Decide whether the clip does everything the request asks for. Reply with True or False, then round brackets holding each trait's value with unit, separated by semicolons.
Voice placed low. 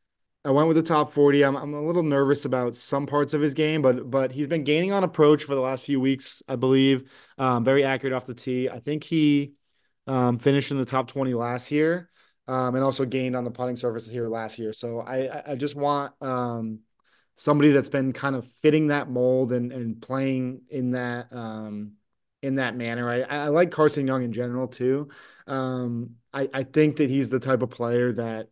True (130 Hz)